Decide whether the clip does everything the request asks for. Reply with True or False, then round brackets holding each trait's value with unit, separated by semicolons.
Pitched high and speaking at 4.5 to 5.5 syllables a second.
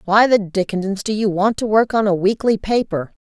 True (205 Hz; 5.3 syllables/s)